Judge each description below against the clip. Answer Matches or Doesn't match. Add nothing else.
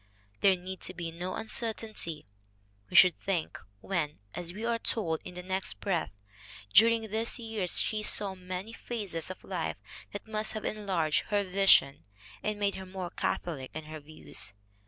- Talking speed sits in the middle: Matches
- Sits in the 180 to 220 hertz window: Matches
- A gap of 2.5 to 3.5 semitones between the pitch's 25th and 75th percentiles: Doesn't match